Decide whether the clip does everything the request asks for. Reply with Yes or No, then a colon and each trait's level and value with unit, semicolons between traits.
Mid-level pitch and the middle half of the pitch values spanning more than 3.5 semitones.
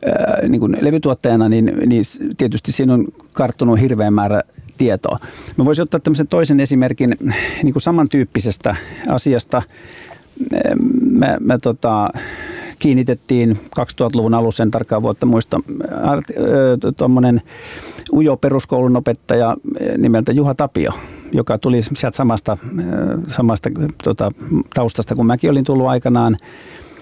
No: low, 125 Hz; average, 4.2 semitones